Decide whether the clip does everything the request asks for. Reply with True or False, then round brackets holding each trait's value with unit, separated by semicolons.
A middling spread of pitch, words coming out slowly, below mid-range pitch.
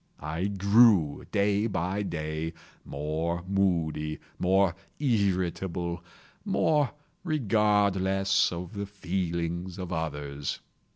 True (3.2 semitones; 90 wpm; 95 Hz)